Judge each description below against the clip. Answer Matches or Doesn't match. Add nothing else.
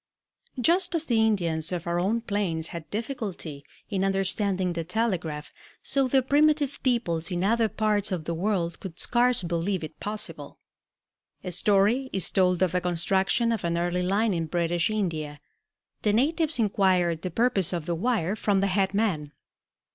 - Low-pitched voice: Doesn't match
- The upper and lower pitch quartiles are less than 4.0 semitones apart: Doesn't match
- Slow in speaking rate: Doesn't match